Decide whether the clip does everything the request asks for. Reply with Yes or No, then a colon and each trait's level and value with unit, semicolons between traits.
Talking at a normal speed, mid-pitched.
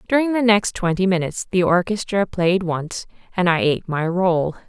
Yes: average, 180 wpm; medium, 180 Hz